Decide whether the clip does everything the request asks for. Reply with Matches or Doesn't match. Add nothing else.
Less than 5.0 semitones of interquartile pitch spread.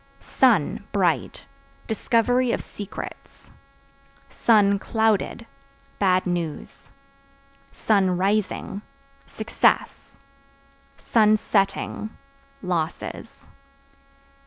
Matches